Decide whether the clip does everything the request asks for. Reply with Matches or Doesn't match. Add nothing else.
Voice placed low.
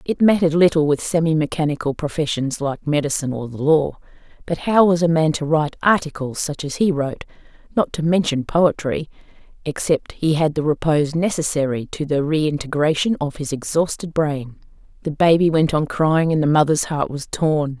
Doesn't match